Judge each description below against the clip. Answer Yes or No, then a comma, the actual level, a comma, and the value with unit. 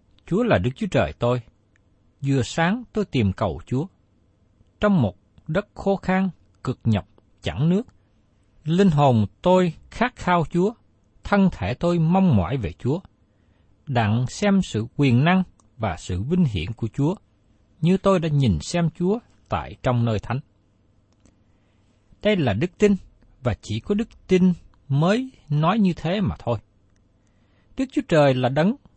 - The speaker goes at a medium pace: No, slow, 155 wpm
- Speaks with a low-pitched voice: Yes, low, 120 Hz